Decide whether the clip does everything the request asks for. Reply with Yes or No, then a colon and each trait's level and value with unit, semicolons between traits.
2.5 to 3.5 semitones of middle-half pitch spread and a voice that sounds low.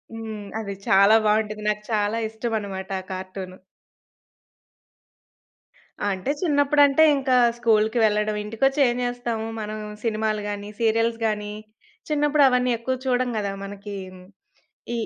No: average, 2.9 semitones; high, 220 Hz